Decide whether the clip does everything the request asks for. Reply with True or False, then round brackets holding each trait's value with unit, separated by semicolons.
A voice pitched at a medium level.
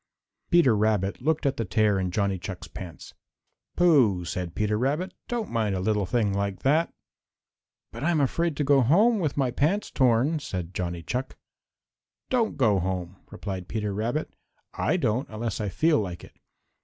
False (110 Hz)